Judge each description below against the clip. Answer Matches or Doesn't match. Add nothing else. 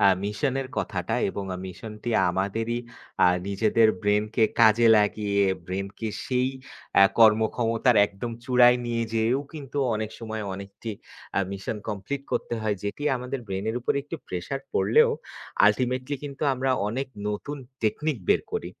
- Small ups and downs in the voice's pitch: Doesn't match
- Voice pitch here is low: Matches